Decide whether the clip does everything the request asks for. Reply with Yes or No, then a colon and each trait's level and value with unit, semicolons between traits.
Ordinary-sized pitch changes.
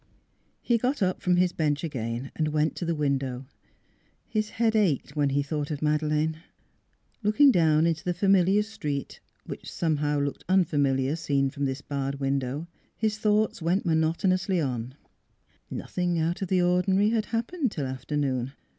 Yes: average, 5.0 semitones